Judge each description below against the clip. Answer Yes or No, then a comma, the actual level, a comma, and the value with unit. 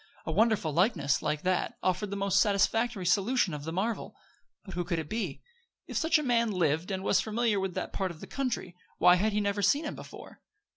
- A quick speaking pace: Yes, fast, 215 wpm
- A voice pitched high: Yes, high, 195 Hz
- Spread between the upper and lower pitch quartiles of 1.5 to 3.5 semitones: No, average, 4.0 semitones